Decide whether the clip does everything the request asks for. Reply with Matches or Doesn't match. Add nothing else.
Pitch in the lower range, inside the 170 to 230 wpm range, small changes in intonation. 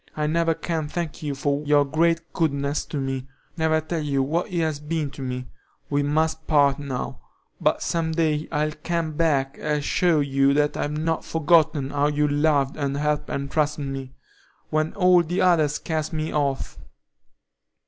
Doesn't match